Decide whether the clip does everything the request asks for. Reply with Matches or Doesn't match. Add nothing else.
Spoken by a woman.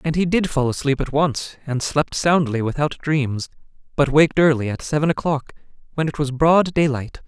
Doesn't match